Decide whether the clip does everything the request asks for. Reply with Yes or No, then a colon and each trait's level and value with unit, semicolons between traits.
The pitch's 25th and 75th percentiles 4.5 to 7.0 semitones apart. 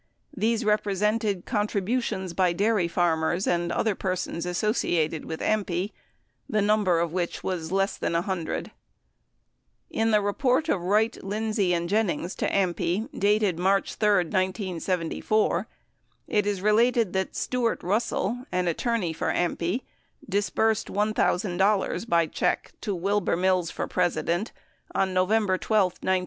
No: average, 3.2 semitones